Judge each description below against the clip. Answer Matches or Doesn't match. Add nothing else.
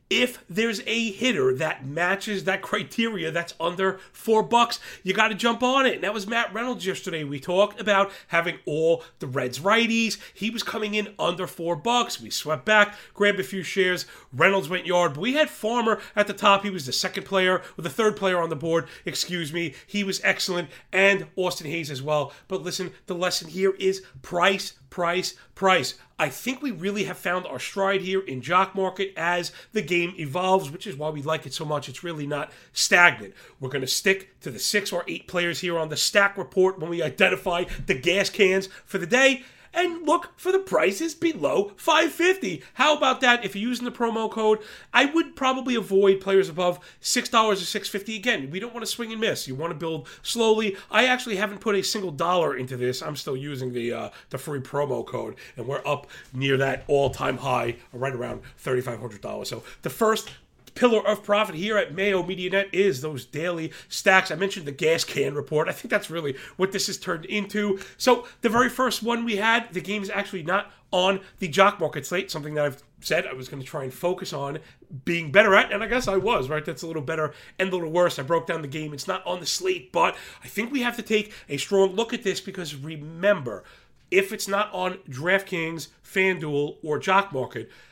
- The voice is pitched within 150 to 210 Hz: Matches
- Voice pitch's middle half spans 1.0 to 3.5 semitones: Doesn't match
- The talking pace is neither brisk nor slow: Doesn't match